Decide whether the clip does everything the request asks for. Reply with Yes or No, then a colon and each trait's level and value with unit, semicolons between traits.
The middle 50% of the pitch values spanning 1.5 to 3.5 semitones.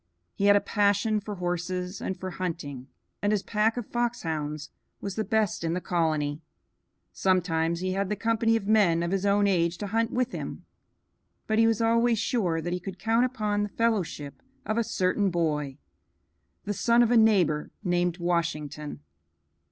No: average, 4.3 semitones